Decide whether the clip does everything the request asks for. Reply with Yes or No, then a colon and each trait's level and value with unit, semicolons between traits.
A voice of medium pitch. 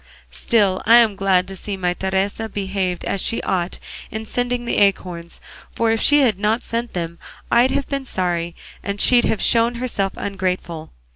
No: high, 200 Hz